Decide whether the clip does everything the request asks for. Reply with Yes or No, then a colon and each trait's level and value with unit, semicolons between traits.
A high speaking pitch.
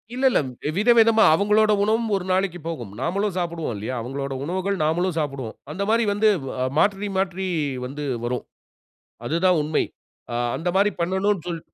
No: medium, 180 Hz